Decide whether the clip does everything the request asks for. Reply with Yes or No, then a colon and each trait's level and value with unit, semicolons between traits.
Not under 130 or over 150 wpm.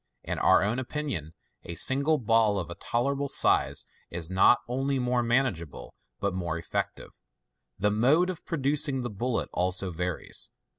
Yes: average, 145 wpm